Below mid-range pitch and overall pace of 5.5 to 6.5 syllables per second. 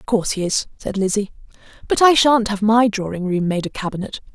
No: high, 210 Hz; 6.0 syllables/s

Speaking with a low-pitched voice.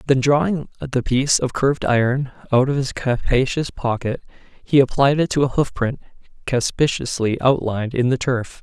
Yes: low, 130 Hz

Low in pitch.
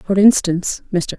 No: medium, 185 Hz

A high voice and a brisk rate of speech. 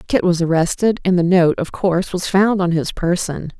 No: medium, 180 Hz; fast, 215 wpm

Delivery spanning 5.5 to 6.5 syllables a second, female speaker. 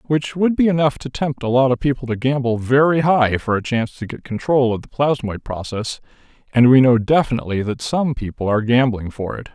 No: 5.6 syllables/s; male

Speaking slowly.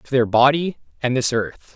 No: fast, 205 wpm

